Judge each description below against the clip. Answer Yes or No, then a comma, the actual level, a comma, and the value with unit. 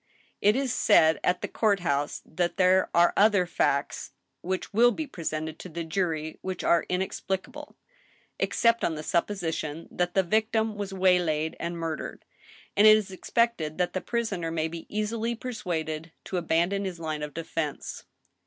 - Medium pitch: Yes, medium, 180 Hz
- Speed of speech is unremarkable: Yes, average, 165 wpm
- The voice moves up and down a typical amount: Yes, average, 4.3 semitones